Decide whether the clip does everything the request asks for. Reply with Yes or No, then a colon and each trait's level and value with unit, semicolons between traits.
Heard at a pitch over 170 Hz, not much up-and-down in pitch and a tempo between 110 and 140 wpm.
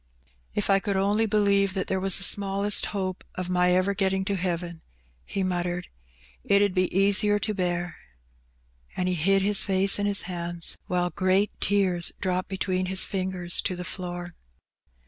No: high, 190 Hz; narrow, 1.7 semitones; average, 175 wpm